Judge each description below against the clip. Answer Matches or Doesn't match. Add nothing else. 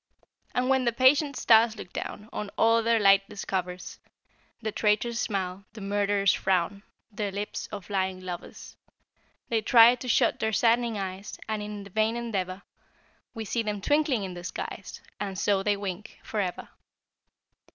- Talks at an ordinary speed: Matches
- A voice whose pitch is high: Matches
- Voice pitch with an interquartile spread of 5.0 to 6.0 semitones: Doesn't match